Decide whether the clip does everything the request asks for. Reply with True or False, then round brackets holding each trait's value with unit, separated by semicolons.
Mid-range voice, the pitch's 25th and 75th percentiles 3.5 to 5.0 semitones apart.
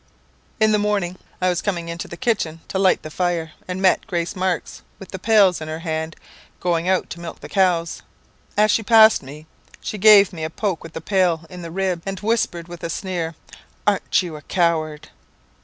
False (180 Hz; 2.8 semitones)